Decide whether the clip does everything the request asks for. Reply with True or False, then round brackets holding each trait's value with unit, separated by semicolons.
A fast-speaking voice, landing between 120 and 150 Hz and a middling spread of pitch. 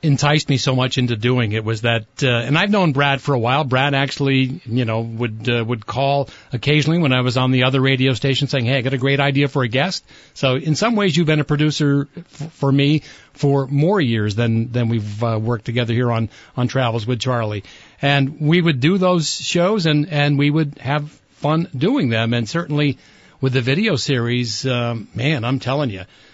True (215 wpm; 135 Hz; 3.4 semitones)